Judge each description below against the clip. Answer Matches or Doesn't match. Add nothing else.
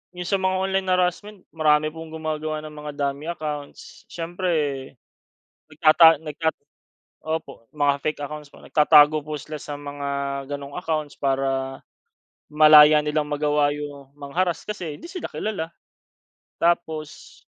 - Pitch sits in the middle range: Matches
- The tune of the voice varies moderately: Doesn't match